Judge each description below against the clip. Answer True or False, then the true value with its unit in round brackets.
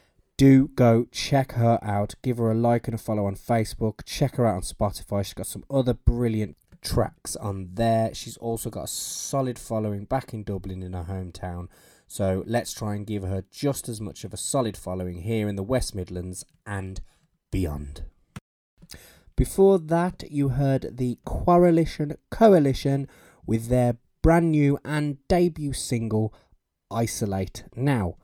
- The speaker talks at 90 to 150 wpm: False (160 wpm)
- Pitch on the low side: True (115 Hz)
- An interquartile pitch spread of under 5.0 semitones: False (5.5 semitones)